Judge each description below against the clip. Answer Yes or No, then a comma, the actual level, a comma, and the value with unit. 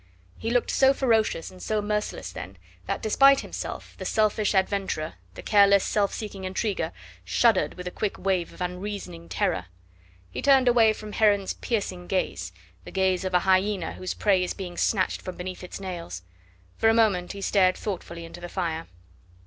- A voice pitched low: No, high, 190 Hz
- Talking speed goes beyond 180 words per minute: No, average, 175 wpm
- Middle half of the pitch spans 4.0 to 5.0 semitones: No, average, 2.9 semitones